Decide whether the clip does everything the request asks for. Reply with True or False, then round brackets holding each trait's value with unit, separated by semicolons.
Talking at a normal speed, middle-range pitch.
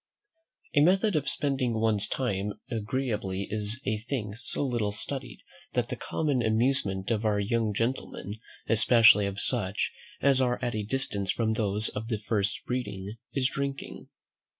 False (150 wpm; 110 Hz)